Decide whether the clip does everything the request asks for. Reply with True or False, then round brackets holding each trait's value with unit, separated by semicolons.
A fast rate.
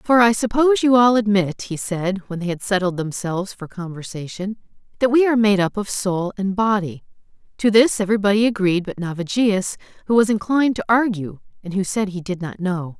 False (195 wpm)